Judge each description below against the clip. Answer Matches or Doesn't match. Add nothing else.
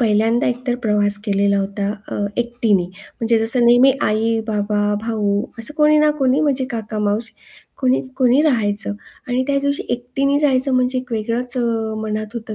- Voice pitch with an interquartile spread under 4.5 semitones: Matches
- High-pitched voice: Matches